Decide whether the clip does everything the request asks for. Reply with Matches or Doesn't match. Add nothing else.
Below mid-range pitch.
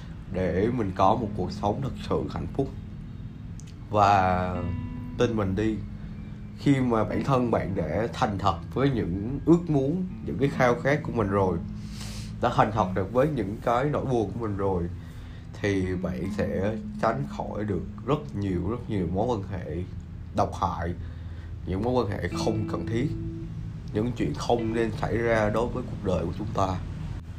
Matches